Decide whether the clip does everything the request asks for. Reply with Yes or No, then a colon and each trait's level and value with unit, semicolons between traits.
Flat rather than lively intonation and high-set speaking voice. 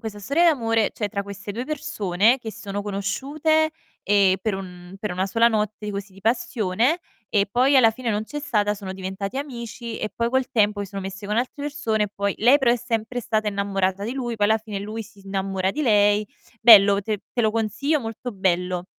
No: average, 3.2 semitones; high, 215 Hz